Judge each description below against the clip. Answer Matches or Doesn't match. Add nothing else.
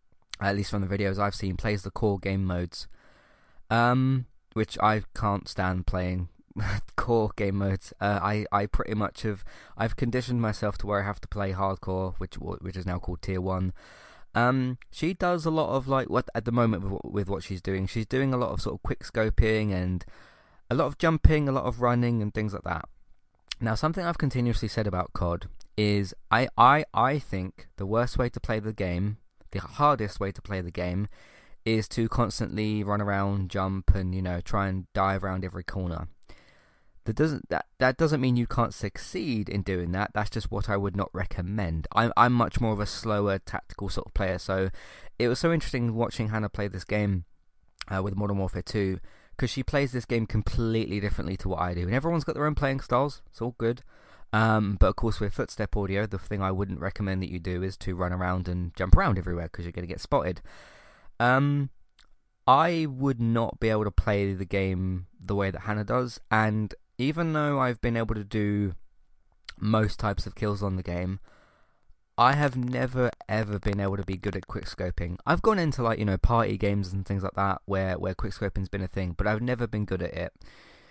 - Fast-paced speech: Matches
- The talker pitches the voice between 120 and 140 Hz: Doesn't match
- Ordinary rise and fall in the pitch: Matches